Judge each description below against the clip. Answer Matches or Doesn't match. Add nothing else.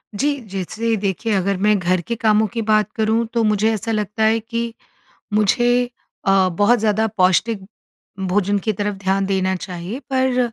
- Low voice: Doesn't match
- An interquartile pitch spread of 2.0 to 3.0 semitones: Matches